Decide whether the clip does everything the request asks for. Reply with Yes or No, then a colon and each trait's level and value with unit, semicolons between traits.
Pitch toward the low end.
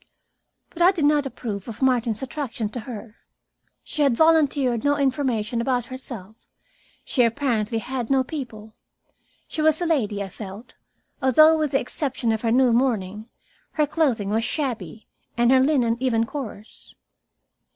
No: very high, 250 Hz